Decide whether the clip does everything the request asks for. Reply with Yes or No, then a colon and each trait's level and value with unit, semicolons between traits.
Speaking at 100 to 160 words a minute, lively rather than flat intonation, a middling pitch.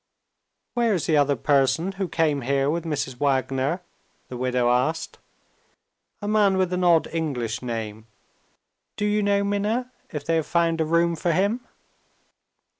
Yes: average, 155 wpm; wide, 6.0 semitones; medium, 165 Hz